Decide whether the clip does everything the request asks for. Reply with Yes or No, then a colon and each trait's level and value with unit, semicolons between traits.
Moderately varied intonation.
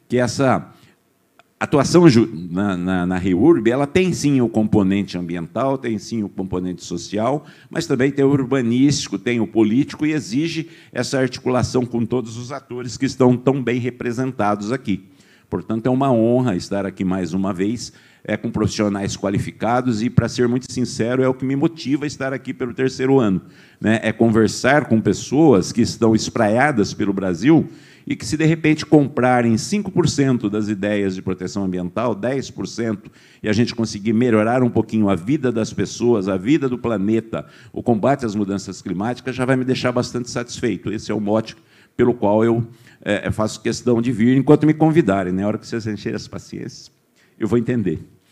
Yes: average, 4.0 semitones